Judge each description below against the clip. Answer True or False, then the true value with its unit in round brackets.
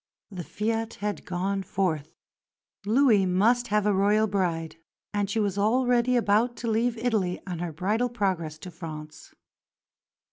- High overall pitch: True (205 Hz)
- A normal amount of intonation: True (3.9 semitones)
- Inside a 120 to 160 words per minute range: True (145 wpm)